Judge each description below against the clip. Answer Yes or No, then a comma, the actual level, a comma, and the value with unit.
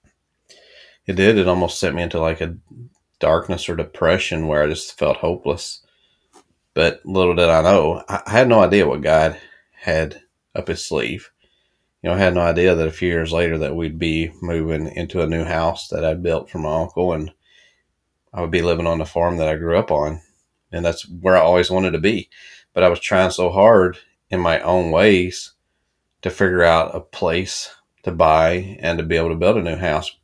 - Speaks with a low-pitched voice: Yes, very low, 85 Hz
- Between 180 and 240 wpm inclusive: Yes, fast, 205 wpm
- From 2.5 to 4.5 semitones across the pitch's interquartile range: No, narrow, 2.0 semitones